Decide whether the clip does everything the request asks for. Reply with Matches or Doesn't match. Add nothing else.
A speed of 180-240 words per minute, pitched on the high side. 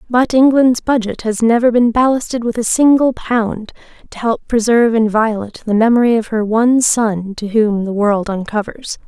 Doesn't match